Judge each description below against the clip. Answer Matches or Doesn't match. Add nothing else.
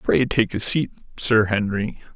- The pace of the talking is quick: Doesn't match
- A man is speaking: Matches